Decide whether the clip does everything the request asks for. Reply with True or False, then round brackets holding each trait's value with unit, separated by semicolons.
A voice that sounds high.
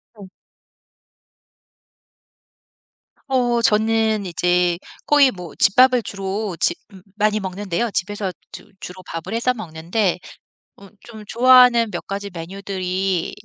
True (200 Hz)